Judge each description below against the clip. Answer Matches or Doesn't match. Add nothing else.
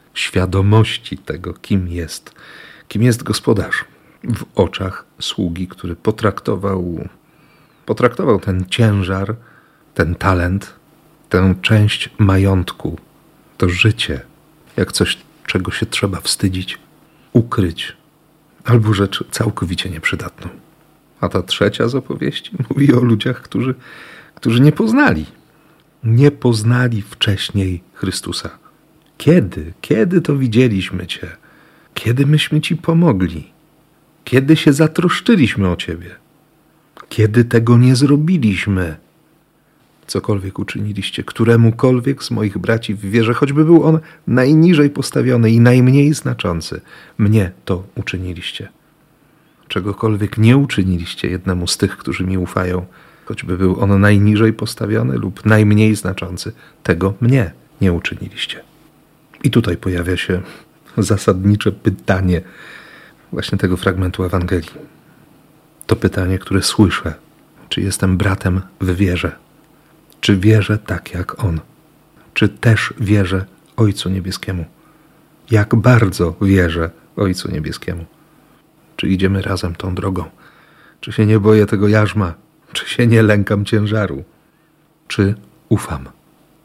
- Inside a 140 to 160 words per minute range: Doesn't match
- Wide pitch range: Matches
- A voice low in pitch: Matches